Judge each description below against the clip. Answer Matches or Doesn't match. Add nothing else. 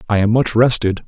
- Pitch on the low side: Matches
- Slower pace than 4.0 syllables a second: Doesn't match